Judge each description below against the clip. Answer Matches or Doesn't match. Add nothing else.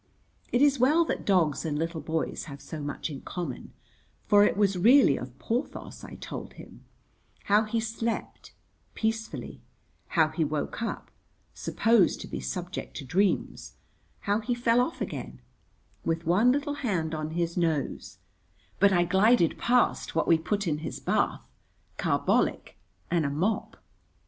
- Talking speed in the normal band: Matches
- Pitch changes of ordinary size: Doesn't match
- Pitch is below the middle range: Doesn't match